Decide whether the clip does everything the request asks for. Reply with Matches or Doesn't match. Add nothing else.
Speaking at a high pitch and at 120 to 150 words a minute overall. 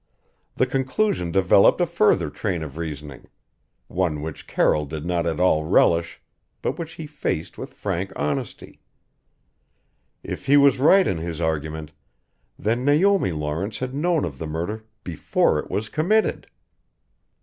Doesn't match